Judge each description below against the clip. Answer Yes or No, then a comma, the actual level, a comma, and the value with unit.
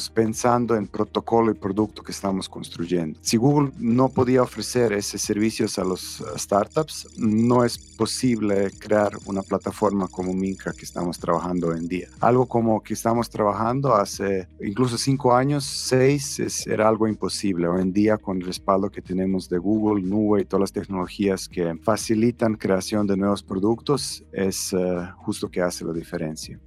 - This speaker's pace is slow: No, average, 165 wpm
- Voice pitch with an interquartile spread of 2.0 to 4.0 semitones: Yes, average, 3.4 semitones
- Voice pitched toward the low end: Yes, low, 100 Hz